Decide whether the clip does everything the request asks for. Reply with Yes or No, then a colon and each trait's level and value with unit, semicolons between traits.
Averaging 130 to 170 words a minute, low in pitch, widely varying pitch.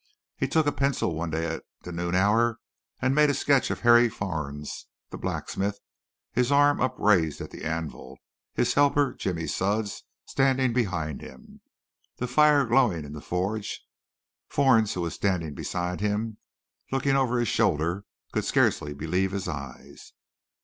Yes: average, 155 wpm; low, 100 Hz; wide, 7.3 semitones